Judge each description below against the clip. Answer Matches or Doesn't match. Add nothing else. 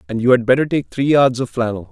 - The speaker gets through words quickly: Matches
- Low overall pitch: Matches